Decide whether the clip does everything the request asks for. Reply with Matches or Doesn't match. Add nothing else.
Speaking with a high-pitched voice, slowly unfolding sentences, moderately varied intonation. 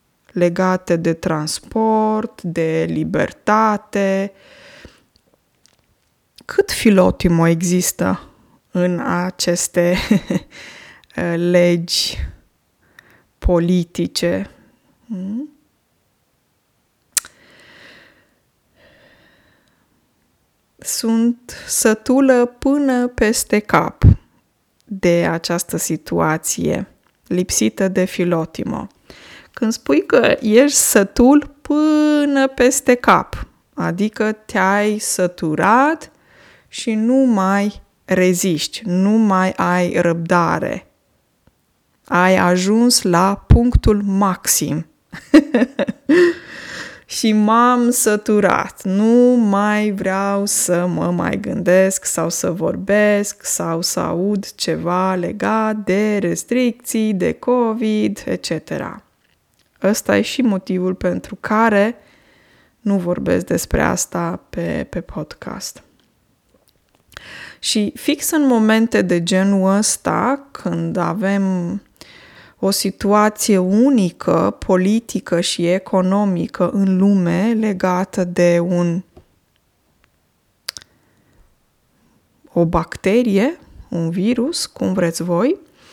Matches